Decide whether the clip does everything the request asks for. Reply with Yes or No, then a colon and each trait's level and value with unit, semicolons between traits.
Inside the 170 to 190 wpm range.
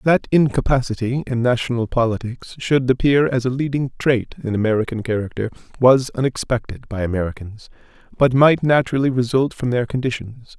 No: average, 140 wpm